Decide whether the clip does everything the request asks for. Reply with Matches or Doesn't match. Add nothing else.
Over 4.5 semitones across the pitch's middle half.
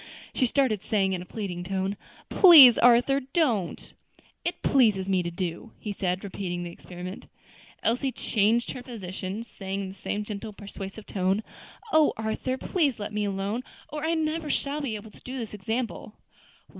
Matches